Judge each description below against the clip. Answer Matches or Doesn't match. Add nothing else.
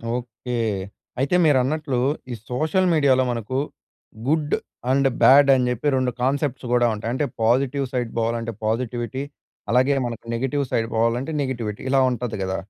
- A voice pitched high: Doesn't match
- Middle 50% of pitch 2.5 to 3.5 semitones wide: Matches